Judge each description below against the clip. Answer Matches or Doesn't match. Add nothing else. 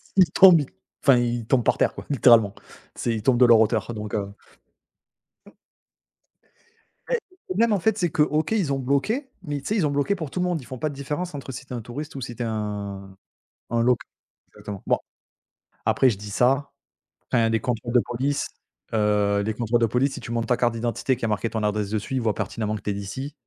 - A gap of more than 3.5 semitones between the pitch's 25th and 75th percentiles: Matches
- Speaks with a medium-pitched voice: Doesn't match